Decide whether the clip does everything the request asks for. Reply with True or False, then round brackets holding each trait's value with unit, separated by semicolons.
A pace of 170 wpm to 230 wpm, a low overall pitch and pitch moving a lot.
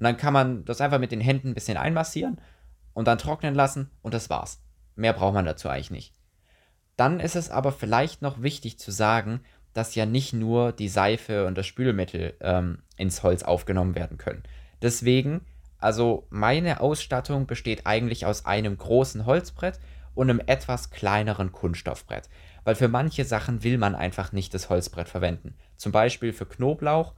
True (175 wpm; 110 Hz; 5.7 semitones)